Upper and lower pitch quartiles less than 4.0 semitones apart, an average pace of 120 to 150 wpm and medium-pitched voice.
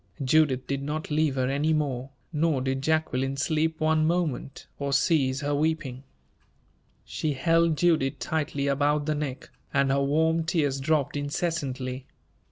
Yes: average, 2.7 semitones; average, 145 wpm; medium, 145 Hz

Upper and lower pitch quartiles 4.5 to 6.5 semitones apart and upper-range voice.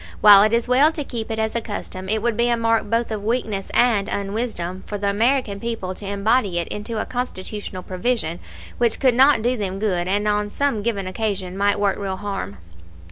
No: average, 3.0 semitones; high, 210 Hz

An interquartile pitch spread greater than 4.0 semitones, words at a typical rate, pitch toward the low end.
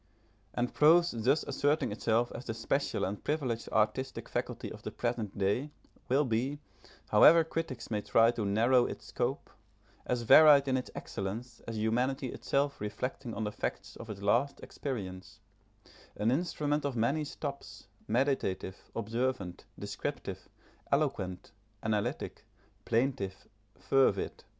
No: average, 4.5 semitones; slow, 130 wpm; low, 120 Hz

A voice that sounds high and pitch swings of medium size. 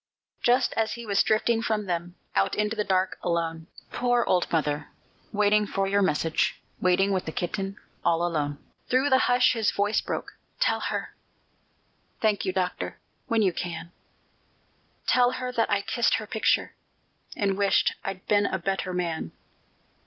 Yes: high, 200 Hz; average, 4.1 semitones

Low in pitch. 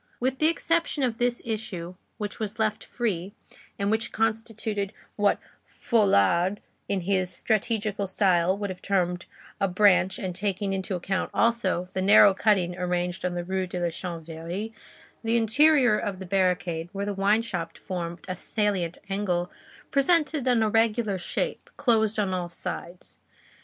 No: high, 200 Hz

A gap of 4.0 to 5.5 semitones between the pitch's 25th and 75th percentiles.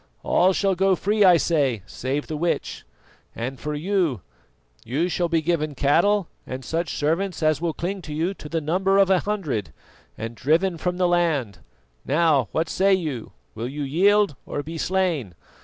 Yes: average, 4.4 semitones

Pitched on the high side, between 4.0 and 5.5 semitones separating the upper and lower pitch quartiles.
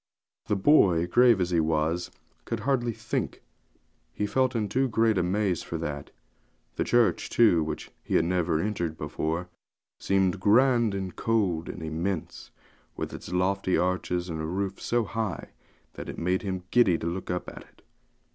No: very low, 95 Hz; average, 4.4 semitones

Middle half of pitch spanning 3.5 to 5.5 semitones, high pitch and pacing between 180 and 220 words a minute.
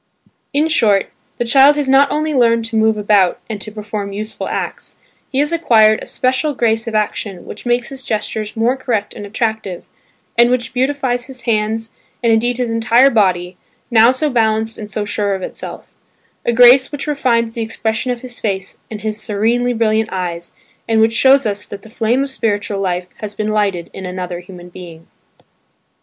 No: average, 3.1 semitones; high, 225 Hz; average, 190 wpm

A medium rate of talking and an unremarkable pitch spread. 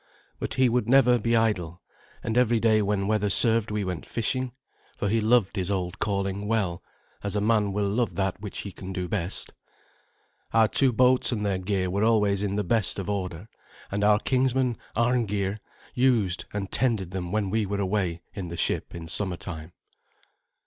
Yes: average, 185 wpm; average, 3.1 semitones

